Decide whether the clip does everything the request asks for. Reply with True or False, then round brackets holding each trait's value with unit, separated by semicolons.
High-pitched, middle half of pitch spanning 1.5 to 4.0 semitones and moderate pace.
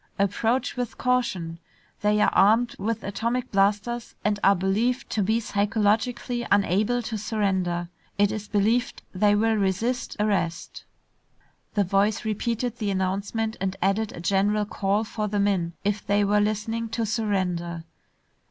True (210 Hz; 2.4 semitones; 145 wpm)